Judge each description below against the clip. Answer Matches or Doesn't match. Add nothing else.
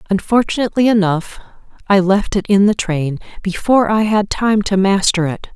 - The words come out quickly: Doesn't match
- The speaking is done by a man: Doesn't match